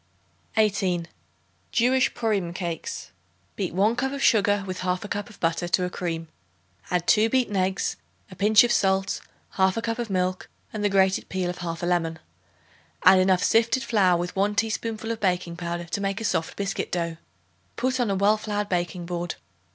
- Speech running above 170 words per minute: Yes, average, 180 wpm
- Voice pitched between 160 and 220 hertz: Yes, high, 190 Hz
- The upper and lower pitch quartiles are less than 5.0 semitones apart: Yes, average, 3.2 semitones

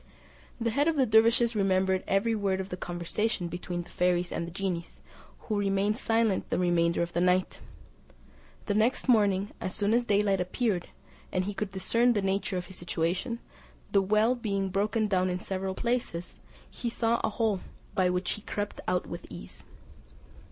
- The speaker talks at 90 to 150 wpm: No, average, 180 wpm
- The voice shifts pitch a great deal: No, average, 3.4 semitones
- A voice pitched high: Yes, high, 195 Hz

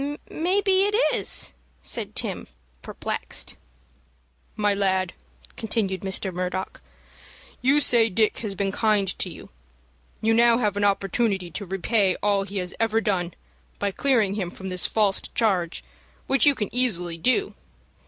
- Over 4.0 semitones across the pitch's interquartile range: No, average, 3.3 semitones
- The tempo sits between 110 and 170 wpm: Yes, average, 145 wpm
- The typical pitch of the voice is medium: No, high, 205 Hz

